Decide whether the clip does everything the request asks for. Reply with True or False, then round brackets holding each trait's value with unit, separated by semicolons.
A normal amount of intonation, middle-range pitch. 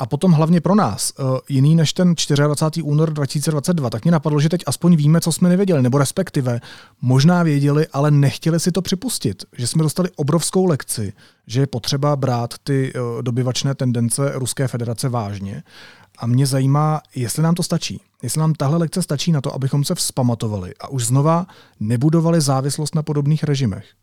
True (4.4 semitones; 145 Hz)